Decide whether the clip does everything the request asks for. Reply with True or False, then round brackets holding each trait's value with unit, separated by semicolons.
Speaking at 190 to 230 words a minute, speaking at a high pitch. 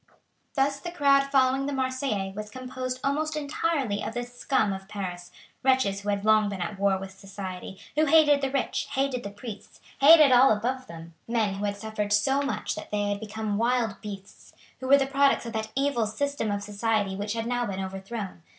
True (200 wpm; 225 Hz)